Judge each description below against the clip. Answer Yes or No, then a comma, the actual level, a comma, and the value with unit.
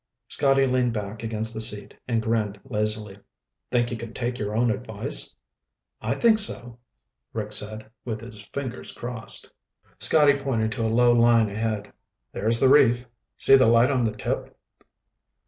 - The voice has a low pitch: Yes, low, 115 Hz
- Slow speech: No, average, 160 wpm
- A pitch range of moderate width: No, narrow, 2.3 semitones